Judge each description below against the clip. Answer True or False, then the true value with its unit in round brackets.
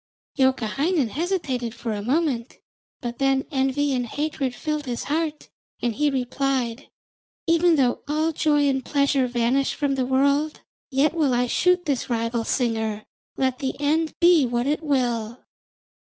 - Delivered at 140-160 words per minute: True (150 wpm)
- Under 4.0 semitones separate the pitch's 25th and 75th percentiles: True (3.6 semitones)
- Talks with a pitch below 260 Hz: False (270 Hz)